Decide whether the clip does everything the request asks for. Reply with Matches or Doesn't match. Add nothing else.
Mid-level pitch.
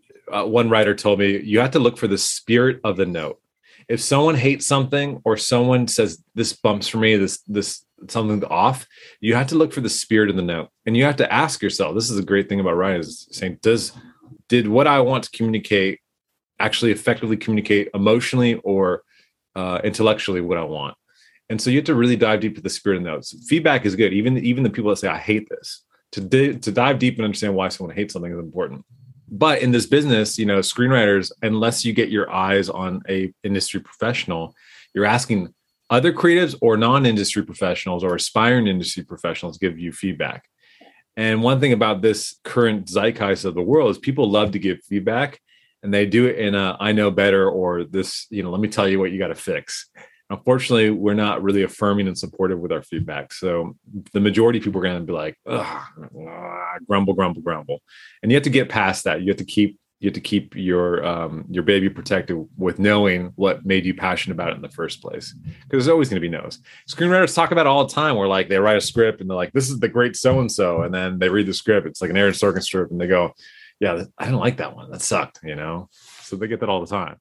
Doesn't match